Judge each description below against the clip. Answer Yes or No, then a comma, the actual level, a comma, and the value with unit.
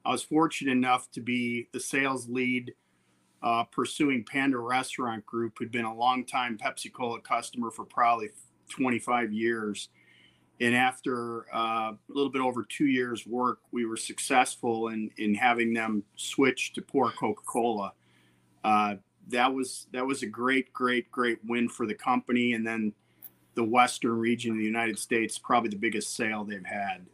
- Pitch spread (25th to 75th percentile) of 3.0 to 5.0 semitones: No, narrow, 2.6 semitones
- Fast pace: No, average, 160 wpm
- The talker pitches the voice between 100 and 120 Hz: Yes, low, 115 Hz